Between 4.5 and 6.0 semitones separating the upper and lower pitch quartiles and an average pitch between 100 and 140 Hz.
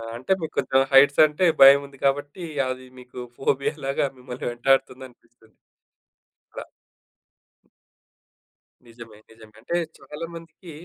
No: average, 2.7 semitones; low, 135 Hz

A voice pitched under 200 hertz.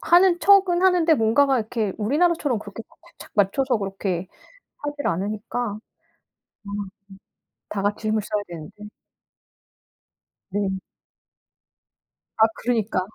No: high, 220 Hz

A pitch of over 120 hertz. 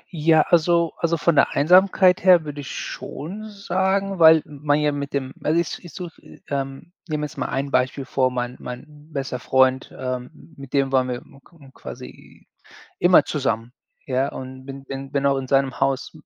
Yes: medium, 140 Hz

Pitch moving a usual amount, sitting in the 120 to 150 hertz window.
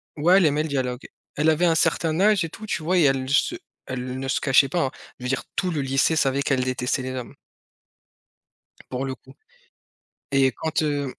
Yes: average, 3.5 semitones; medium, 140 Hz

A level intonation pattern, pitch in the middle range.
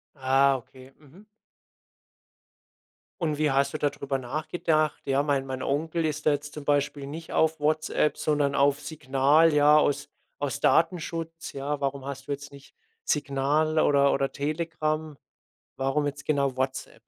Yes: narrow, 2.0 semitones; medium, 145 Hz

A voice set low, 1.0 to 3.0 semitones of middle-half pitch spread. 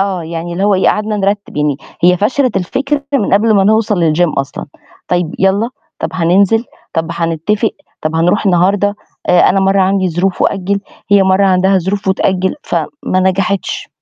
No: high, 190 Hz; narrow, 2.4 semitones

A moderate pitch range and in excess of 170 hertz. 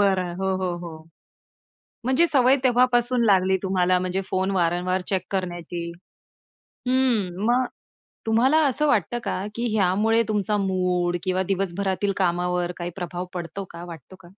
Yes: average, 3.9 semitones; high, 190 Hz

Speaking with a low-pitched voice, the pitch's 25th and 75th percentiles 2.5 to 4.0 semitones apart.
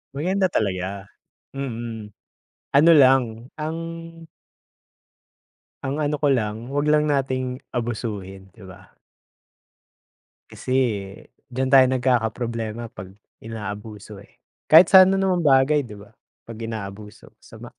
No: low, 120 Hz; average, 5.0 semitones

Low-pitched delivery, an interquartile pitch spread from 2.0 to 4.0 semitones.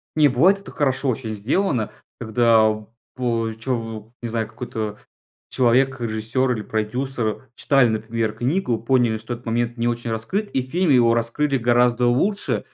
Yes: low, 120 Hz; average, 2.9 semitones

